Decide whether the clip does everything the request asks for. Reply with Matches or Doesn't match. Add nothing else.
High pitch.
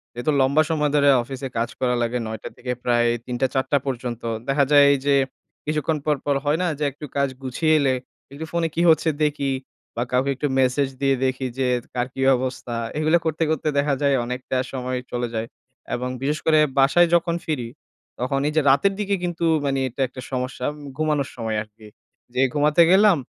Doesn't match